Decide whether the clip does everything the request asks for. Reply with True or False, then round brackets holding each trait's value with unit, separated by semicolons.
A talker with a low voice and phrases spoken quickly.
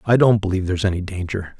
True (95 Hz; 225 wpm)